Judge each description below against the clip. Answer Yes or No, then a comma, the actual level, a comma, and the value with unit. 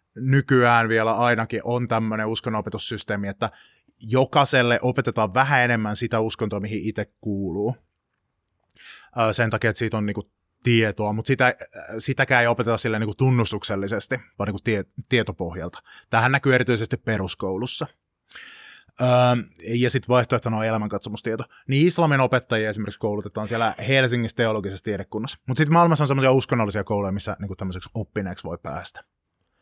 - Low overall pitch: Yes, low, 115 Hz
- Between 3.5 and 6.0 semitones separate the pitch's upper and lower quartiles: No, average, 3.0 semitones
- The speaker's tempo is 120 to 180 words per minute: Yes, average, 130 wpm